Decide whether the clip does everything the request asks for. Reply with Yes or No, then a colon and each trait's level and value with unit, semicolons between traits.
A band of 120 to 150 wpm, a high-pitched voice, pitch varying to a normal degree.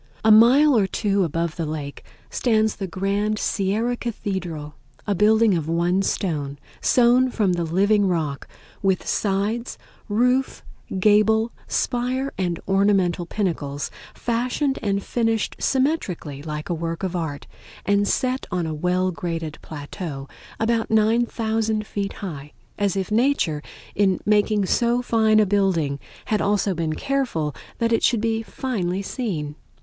Yes: average, 140 wpm; high, 200 Hz; average, 4.8 semitones